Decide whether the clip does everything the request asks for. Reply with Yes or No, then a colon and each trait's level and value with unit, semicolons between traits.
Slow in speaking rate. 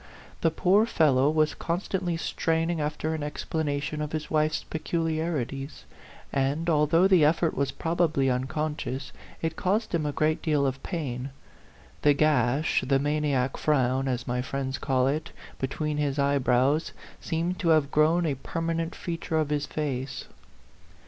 No: average, 150 wpm